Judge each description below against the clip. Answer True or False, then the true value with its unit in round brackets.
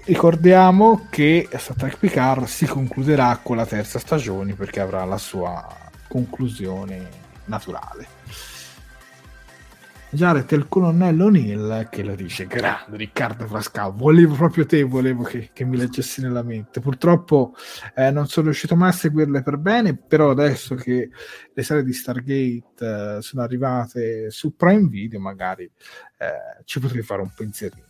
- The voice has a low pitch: True (130 Hz)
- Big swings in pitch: True (6.1 semitones)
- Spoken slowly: False (145 wpm)